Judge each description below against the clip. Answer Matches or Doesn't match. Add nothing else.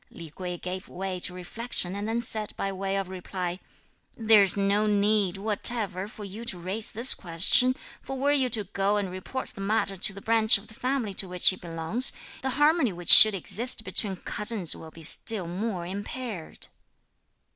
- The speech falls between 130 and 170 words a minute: Doesn't match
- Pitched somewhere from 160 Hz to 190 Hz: Doesn't match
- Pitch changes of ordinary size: Matches